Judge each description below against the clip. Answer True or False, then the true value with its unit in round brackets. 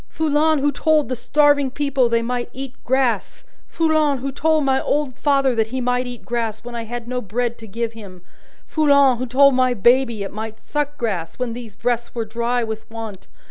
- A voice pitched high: True (245 Hz)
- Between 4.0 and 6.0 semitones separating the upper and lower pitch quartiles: False (3.3 semitones)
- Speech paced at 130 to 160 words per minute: False (200 wpm)